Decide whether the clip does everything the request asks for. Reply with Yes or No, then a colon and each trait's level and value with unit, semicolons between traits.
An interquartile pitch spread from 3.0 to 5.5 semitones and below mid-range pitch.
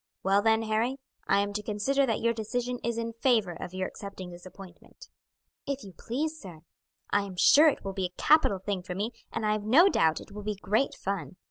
No: average, 3.4 semitones; high, 210 Hz